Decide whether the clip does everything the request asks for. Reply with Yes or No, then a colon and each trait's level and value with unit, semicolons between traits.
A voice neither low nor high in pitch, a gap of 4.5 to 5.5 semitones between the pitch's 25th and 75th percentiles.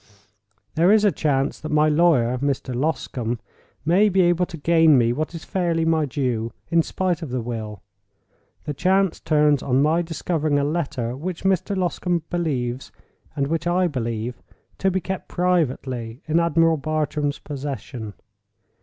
Yes: medium, 155 Hz; average, 4.8 semitones